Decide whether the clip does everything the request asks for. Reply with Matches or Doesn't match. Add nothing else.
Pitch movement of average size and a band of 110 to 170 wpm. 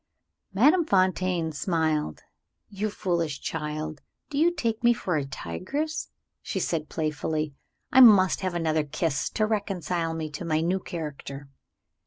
Matches